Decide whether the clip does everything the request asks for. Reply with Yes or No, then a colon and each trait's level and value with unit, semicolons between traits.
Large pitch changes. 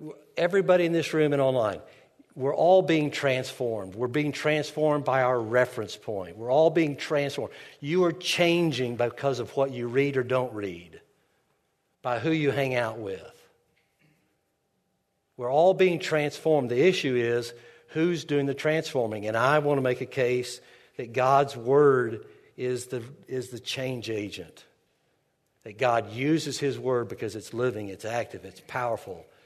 No: average, 4.0 semitones